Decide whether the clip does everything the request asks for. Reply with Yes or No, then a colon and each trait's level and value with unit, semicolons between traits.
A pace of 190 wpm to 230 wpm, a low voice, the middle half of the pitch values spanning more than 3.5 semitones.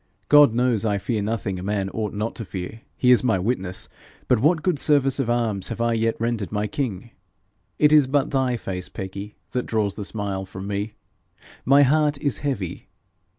Yes: average, 195 wpm; low, 115 Hz; average, 4.6 semitones